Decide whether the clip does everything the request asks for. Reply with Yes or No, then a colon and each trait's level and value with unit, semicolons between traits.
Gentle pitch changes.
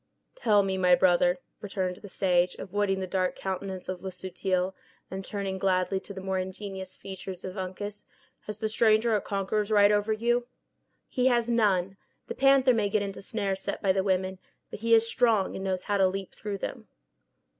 Yes: narrow, 2.1 semitones